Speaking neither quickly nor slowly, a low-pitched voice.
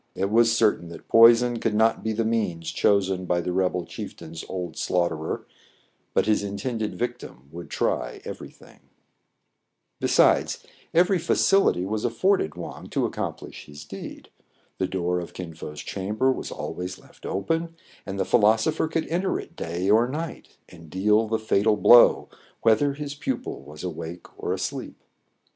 Yes: average, 160 wpm; low, 105 Hz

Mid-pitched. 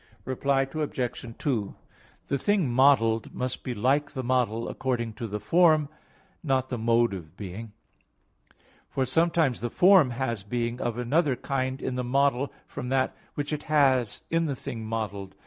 No: low, 130 Hz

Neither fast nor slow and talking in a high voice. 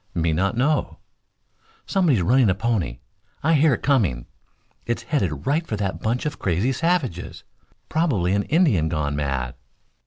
No: average, 150 wpm; low, 110 Hz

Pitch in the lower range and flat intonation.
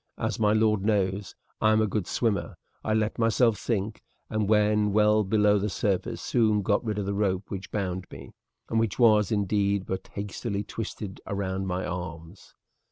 Yes: low, 105 Hz; narrow, 2.0 semitones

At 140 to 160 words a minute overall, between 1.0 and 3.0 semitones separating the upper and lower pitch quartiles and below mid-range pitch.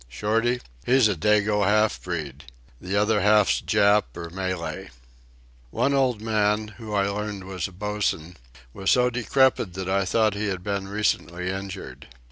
Yes: average, 155 wpm; narrow, 2.4 semitones; low, 100 Hz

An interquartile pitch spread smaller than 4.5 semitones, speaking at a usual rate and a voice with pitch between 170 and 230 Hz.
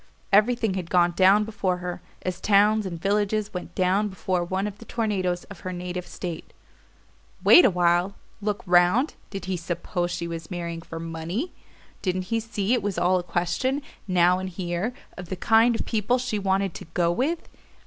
Yes: average, 3.1 semitones; average, 180 wpm; medium, 185 Hz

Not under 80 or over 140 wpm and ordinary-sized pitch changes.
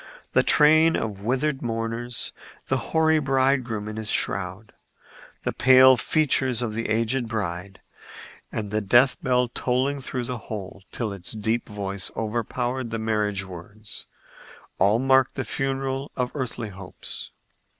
Yes: slow, 135 wpm; average, 3.8 semitones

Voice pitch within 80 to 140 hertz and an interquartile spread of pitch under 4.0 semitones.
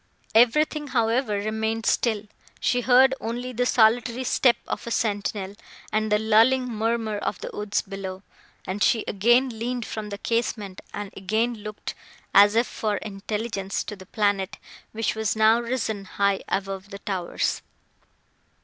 No: high, 220 Hz; narrow, 2.6 semitones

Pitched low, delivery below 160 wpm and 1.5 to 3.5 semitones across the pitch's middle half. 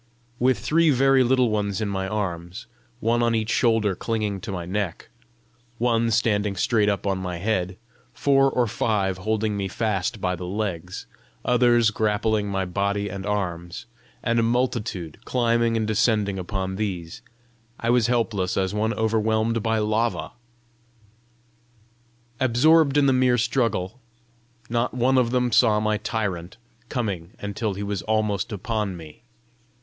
Yes: low, 110 Hz; average, 145 wpm; average, 3.2 semitones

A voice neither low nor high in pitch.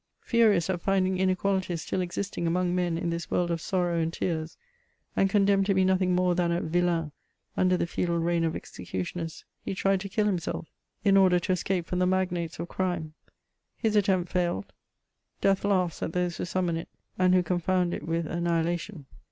Yes: medium, 180 Hz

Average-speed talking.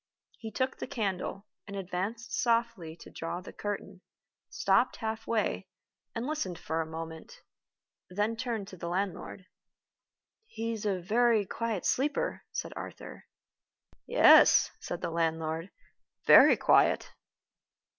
No: slow, 125 wpm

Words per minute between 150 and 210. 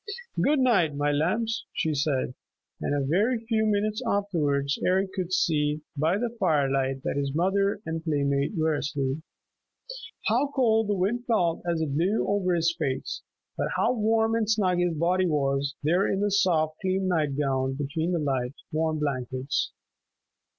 Yes: average, 165 wpm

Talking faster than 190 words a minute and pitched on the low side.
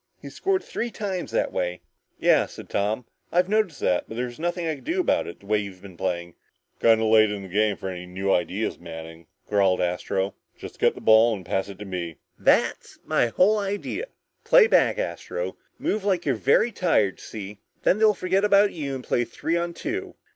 Yes: fast, 205 wpm; low, 110 Hz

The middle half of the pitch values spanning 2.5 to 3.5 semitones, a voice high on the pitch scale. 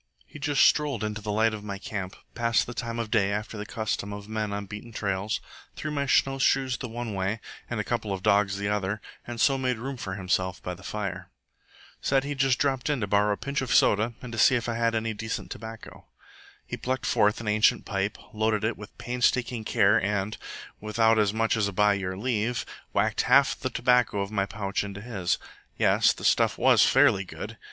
No: average, 2.9 semitones; low, 110 Hz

